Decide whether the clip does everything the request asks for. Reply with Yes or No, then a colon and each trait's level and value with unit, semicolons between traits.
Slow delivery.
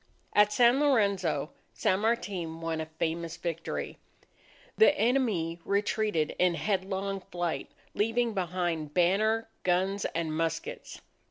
Yes: slow, 110 wpm